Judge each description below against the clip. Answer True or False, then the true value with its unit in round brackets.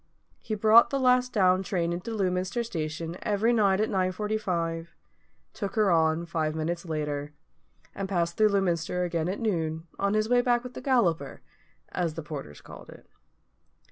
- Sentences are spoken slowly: False (165 wpm)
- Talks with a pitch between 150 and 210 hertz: True (185 Hz)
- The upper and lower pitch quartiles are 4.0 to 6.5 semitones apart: True (4.6 semitones)